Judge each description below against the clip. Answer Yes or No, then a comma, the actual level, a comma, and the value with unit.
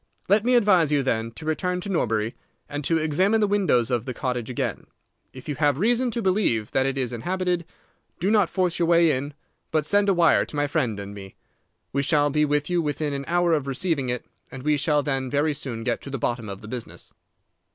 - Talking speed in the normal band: No, fast, 225 wpm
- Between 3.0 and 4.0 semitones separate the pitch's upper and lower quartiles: No, wide, 5.4 semitones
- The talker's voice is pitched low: No, medium, 145 Hz